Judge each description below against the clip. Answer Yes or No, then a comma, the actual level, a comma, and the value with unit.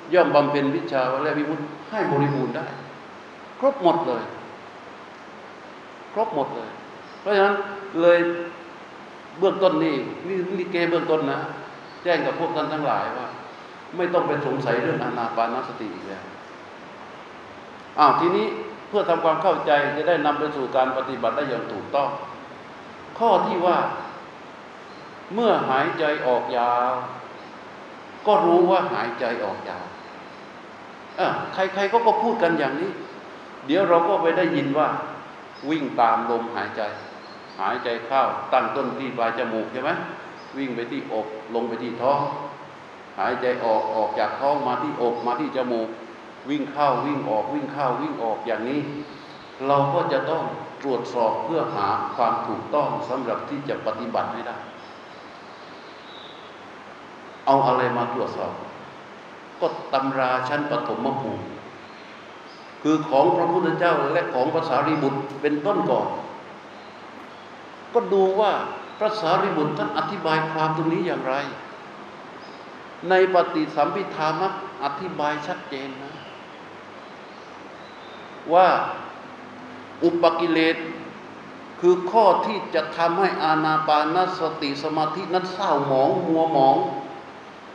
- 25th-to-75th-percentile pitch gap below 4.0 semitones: No, average, 4.3 semitones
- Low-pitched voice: No, medium, 155 Hz